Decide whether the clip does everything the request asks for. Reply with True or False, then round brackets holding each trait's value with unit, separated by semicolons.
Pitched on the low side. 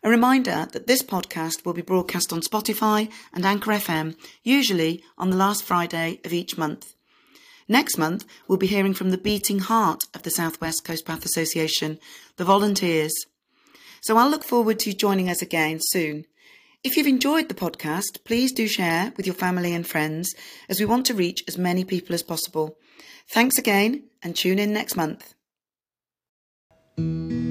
False (185 Hz)